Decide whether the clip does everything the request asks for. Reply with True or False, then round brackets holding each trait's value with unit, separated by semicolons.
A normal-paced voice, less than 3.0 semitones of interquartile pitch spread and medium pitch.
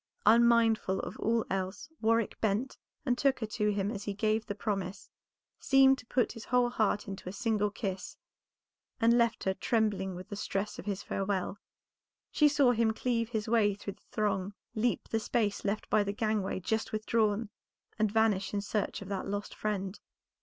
False (180 wpm; 2.4 semitones; 215 Hz)